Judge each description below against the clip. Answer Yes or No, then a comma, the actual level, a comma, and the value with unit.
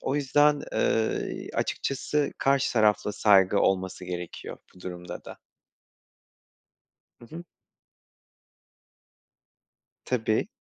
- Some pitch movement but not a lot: No, wide, 6.6 semitones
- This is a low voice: Yes, low, 110 Hz